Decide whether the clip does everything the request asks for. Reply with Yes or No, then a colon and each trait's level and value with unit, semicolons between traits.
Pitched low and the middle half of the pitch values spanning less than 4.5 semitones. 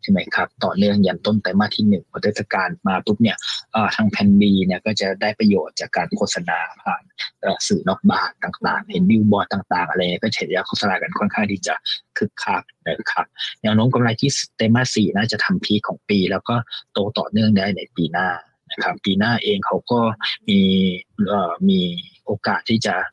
Yes: low, 110 Hz; average, 3.6 semitones